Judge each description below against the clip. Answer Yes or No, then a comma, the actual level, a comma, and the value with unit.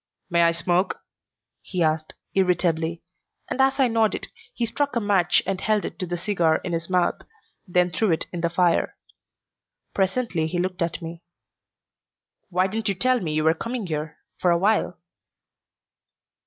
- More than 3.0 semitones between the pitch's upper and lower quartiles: Yes, average, 3.6 semitones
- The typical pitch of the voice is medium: Yes, medium, 180 Hz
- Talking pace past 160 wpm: Yes, average, 170 wpm